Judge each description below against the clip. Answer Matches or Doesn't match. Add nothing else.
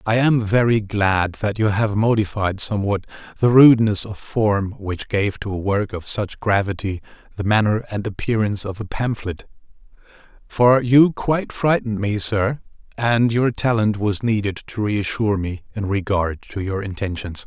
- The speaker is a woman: Doesn't match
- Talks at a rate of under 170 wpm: Matches